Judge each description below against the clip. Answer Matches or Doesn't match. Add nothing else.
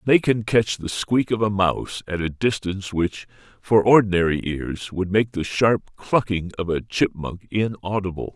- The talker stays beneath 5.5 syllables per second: Matches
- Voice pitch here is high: Doesn't match